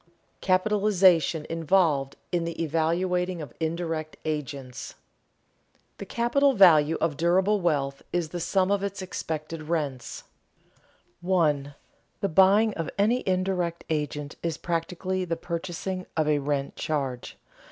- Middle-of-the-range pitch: Yes, medium, 170 Hz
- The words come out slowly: Yes, slow, 125 wpm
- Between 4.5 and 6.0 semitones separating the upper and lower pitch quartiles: No, average, 3.6 semitones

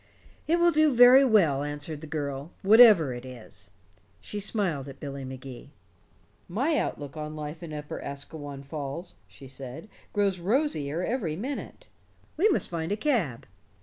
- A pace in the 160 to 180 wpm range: No, average, 150 wpm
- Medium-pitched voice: Yes, medium, 160 Hz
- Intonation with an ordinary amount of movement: No, wide, 7.6 semitones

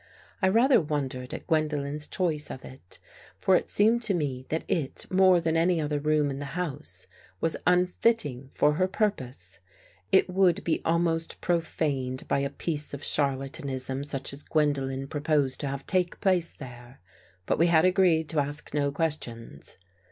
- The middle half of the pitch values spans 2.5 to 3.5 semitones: No, average, 4.1 semitones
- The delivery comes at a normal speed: Yes, average, 165 wpm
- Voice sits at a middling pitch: Yes, medium, 150 Hz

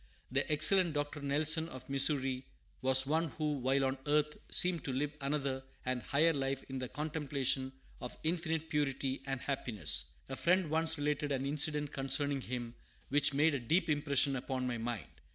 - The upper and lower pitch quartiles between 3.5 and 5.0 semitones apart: No, narrow, 2.4 semitones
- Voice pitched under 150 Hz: Yes, medium, 140 Hz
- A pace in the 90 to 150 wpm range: No, average, 170 wpm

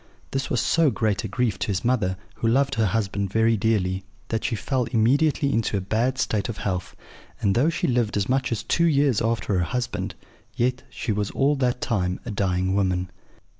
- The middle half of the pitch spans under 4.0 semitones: No, average, 4.4 semitones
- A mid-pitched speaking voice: No, low, 115 Hz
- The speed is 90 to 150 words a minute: No, fast, 205 wpm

